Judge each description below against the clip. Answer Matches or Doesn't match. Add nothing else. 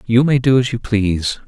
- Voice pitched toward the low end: Matches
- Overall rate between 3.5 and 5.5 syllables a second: Matches